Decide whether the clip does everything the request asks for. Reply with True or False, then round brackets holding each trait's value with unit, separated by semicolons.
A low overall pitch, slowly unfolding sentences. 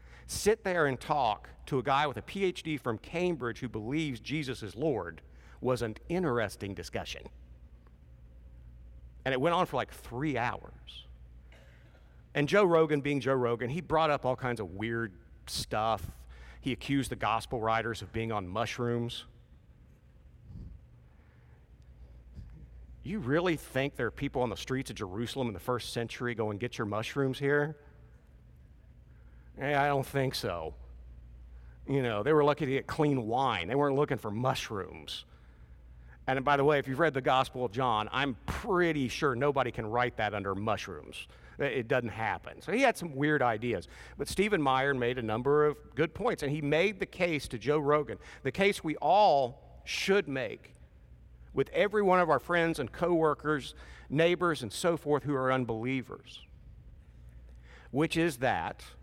False (120 Hz; 165 wpm)